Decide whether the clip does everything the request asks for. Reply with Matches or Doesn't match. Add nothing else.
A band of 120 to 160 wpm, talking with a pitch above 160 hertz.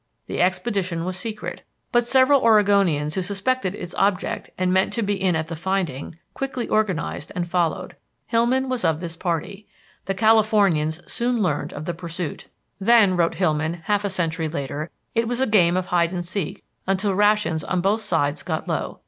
Doesn't match